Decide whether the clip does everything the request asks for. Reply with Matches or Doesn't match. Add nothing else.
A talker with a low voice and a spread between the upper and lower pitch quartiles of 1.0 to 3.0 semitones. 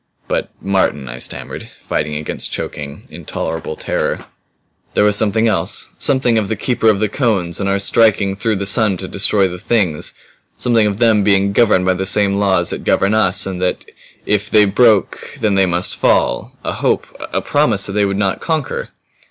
Matches